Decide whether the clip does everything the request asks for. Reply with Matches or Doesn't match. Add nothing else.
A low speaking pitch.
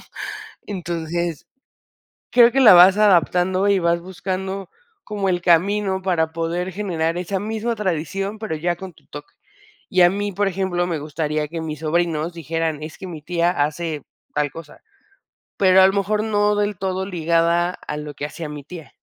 Doesn't match